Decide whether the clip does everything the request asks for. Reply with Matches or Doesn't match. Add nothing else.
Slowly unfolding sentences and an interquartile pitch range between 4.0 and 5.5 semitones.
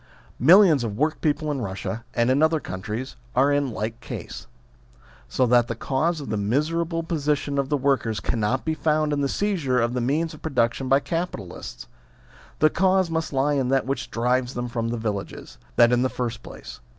Doesn't match